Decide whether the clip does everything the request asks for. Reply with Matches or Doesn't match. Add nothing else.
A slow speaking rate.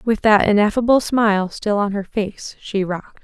Doesn't match